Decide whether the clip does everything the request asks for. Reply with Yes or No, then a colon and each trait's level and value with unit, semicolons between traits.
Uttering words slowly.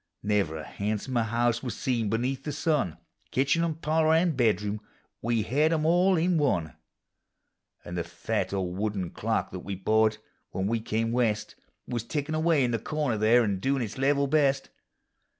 No: average, 180 wpm